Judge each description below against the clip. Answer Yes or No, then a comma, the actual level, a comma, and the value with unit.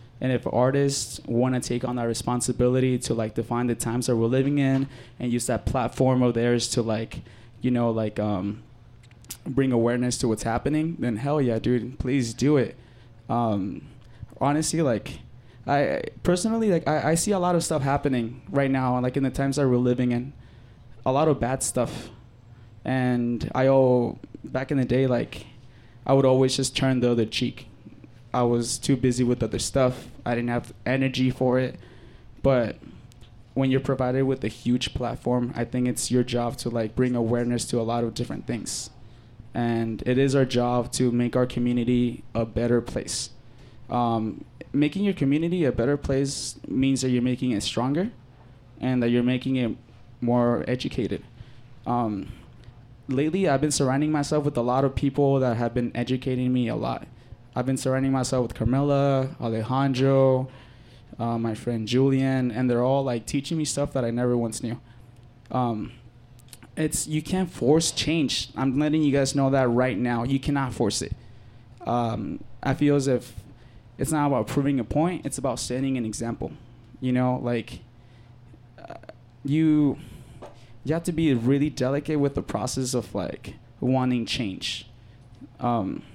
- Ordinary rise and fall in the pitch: No, narrow, 2.2 semitones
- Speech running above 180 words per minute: No, average, 175 wpm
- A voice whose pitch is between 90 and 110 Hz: No, low, 125 Hz